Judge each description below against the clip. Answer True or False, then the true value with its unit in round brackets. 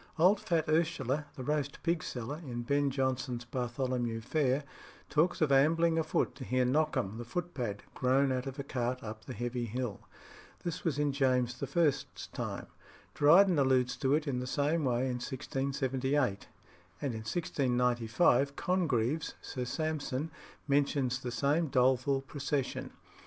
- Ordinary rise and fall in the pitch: True (3.3 semitones)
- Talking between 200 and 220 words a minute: False (145 wpm)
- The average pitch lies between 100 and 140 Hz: True (135 Hz)